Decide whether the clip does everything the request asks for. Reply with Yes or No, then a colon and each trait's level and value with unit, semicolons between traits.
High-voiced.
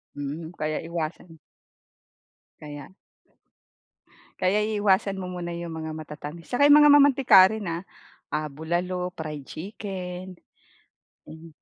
No: medium, 175 Hz